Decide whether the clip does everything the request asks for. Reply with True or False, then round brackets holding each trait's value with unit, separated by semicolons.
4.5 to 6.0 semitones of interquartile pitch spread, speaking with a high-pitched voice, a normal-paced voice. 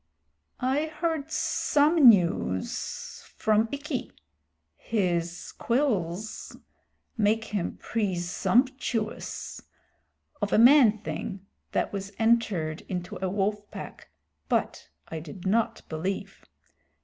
False (5.4 semitones; 210 Hz; 95 wpm)